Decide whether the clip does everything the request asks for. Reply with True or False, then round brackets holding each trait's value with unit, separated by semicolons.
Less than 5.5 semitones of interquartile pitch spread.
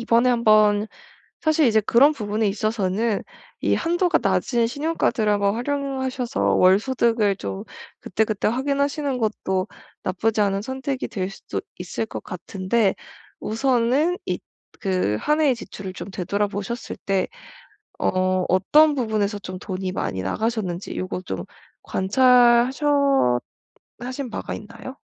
True (5.1 semitones)